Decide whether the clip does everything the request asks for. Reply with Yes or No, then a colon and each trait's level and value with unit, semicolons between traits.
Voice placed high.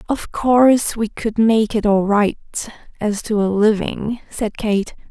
Yes: high, 215 Hz